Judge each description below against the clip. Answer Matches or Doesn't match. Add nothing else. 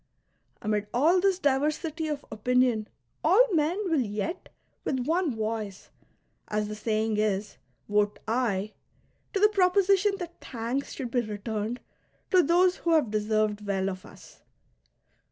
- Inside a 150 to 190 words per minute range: Doesn't match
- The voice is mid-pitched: Doesn't match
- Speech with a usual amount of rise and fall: Doesn't match